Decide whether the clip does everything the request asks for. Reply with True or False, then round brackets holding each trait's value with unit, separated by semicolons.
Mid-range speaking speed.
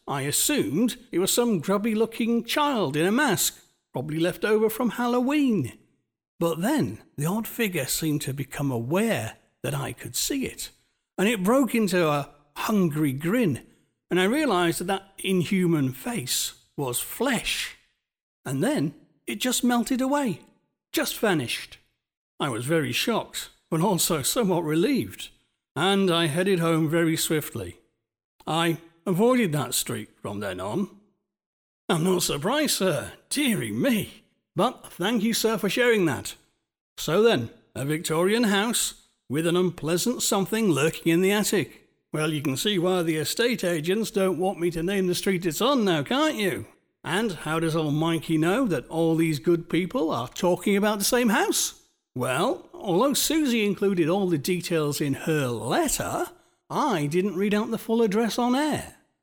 True (160 wpm)